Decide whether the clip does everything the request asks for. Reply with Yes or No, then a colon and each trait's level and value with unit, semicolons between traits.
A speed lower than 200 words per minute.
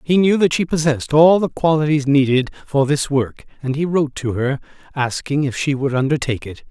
No: fast, 205 wpm